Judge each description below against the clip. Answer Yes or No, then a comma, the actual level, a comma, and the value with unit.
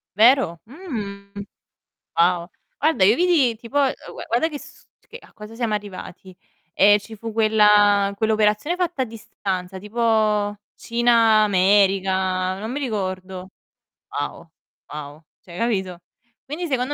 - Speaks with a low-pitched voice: No, high, 210 Hz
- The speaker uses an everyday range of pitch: Yes, average, 3.9 semitones